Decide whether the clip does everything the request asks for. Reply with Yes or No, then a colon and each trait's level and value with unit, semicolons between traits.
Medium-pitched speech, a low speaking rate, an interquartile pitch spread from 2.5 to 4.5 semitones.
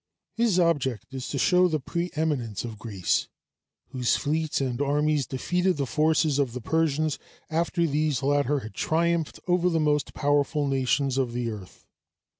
No: medium, 145 Hz; average, 155 wpm; average, 3.7 semitones